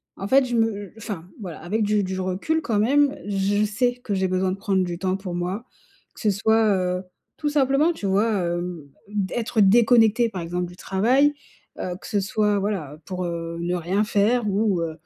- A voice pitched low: No, high, 200 Hz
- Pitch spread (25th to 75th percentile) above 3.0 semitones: Yes, average, 3.6 semitones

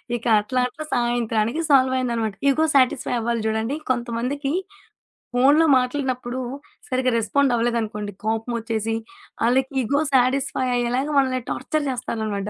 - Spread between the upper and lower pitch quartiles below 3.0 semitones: Yes, narrow, 2.5 semitones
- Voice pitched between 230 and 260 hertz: Yes, high, 245 Hz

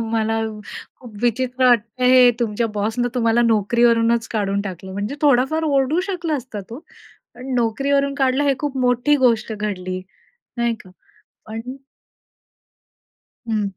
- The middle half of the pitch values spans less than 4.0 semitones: Yes, average, 3.2 semitones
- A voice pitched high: Yes, high, 235 Hz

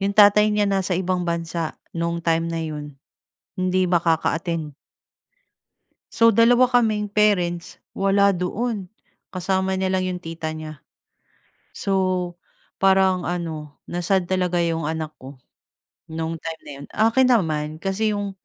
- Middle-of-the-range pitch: Yes, medium, 180 Hz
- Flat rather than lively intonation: No, average, 3.2 semitones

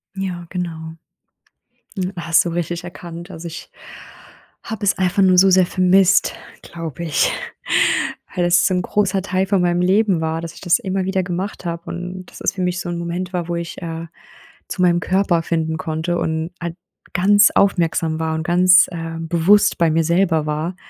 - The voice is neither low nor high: Yes, medium, 175 Hz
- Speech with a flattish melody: Yes, narrow, 2.0 semitones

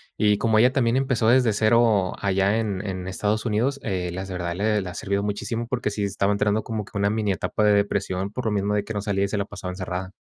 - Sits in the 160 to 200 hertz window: No, low, 105 Hz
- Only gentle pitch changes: Yes, narrow, 2.2 semitones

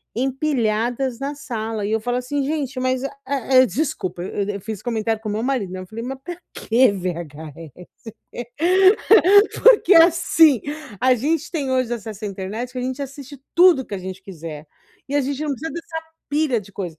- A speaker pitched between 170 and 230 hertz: No, very high, 250 Hz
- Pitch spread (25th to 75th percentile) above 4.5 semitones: Yes, average, 5.3 semitones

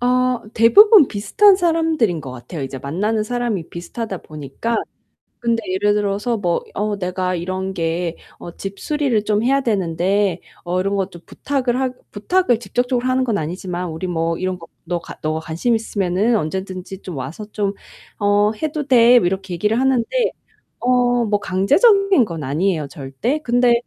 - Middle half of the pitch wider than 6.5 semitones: No, wide, 5.5 semitones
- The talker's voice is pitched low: No, high, 205 Hz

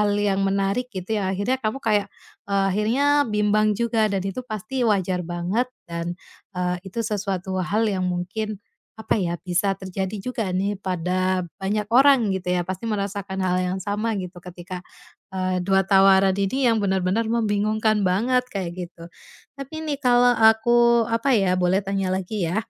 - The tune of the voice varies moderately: Yes, average, 3.1 semitones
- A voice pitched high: Yes, high, 200 Hz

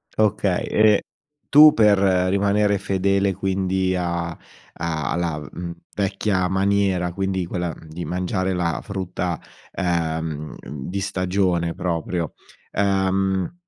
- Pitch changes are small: Yes, narrow, 2.2 semitones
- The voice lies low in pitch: Yes, very low, 95 Hz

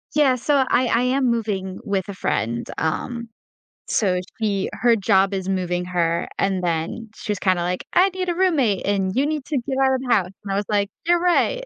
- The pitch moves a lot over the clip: Yes, wide, 5.8 semitones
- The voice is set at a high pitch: Yes, high, 205 Hz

